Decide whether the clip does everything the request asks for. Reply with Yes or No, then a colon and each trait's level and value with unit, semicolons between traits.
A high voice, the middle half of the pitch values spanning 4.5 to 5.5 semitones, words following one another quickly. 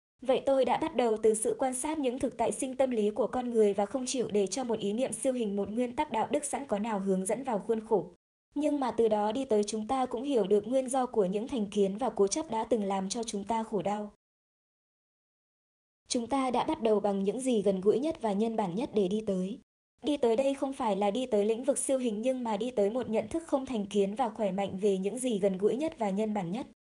No: high, 225 Hz; average, 4.0 semitones; fast, 270 wpm